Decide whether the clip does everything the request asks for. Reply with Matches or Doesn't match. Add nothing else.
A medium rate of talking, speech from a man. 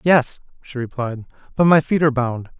Matches